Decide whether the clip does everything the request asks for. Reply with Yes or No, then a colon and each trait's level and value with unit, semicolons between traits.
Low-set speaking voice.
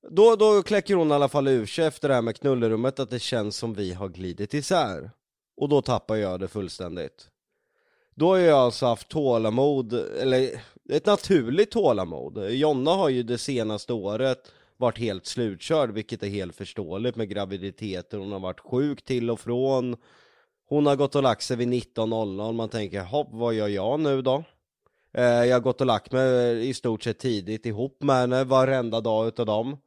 Yes: low, 120 Hz